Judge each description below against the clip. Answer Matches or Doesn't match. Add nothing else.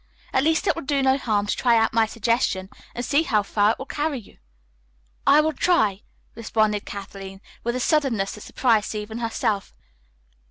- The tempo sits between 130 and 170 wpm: Doesn't match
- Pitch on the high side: Matches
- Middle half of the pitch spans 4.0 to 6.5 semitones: Matches